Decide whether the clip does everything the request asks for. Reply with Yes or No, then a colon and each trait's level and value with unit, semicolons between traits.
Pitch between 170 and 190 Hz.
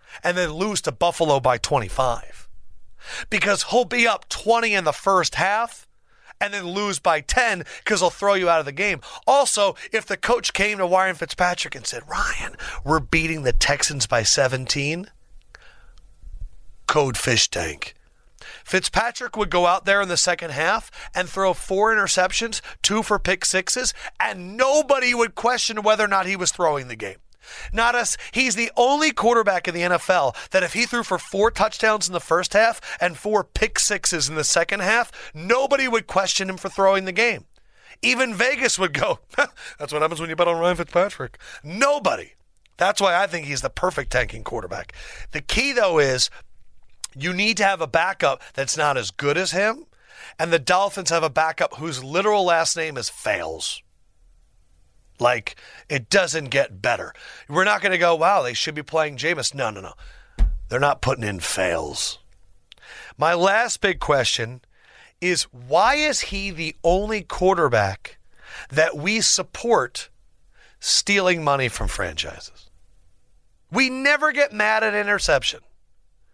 Yes: medium, 185 Hz